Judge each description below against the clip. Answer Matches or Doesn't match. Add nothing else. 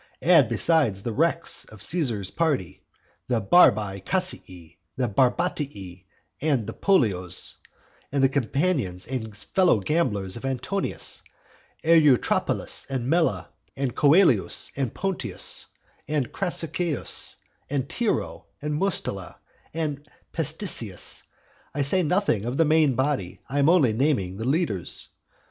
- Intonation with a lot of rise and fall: Matches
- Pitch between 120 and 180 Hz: Matches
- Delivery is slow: Matches